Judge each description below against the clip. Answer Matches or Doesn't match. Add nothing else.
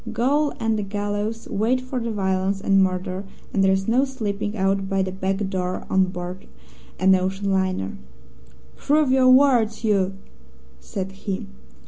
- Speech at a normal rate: Matches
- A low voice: Doesn't match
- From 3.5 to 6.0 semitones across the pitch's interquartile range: Doesn't match